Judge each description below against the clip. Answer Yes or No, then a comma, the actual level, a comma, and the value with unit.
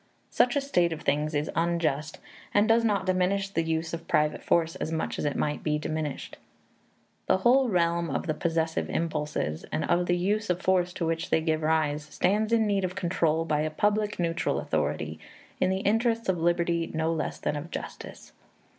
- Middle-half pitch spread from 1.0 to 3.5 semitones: Yes, average, 3.2 semitones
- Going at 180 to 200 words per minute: Yes, average, 195 wpm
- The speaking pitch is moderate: Yes, medium, 170 Hz